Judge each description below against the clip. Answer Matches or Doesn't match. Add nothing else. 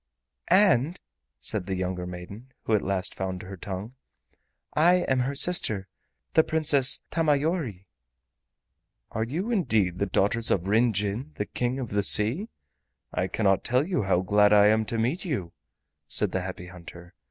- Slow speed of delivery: Doesn't match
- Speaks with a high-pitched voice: Doesn't match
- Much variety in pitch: Matches